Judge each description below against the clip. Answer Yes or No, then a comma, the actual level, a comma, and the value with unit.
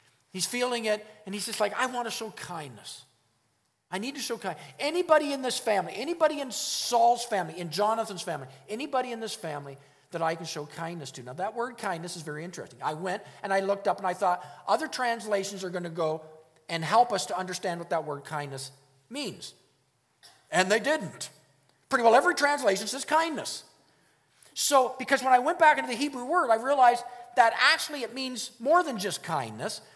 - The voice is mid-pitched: No, high, 215 Hz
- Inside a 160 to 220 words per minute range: Yes, average, 200 wpm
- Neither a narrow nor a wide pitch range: No, wide, 7.0 semitones